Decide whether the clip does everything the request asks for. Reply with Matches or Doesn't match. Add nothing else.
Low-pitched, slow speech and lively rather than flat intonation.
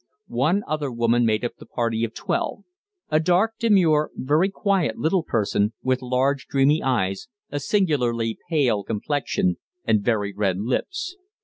Doesn't match